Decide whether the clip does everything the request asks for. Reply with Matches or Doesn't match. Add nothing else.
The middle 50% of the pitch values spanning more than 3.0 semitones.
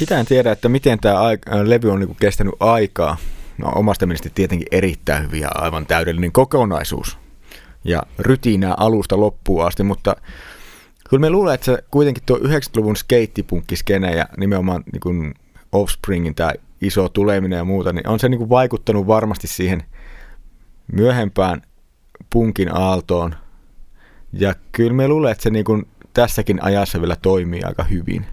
Matches